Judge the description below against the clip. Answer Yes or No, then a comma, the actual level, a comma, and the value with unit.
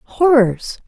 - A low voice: No, very high, 250 Hz